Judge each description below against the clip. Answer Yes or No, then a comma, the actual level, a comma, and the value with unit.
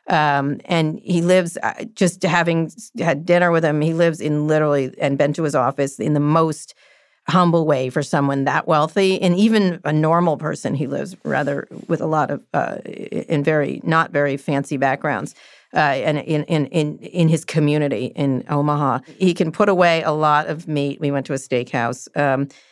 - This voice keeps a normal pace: Yes, average, 190 wpm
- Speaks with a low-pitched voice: No, medium, 155 Hz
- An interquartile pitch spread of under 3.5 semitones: Yes, average, 2.9 semitones